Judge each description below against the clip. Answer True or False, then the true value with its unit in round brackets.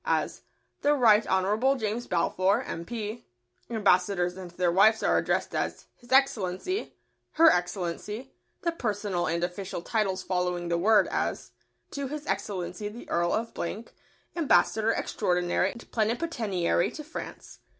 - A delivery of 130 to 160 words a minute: True (140 wpm)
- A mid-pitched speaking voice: False (210 Hz)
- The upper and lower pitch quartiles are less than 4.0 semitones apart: False (5.0 semitones)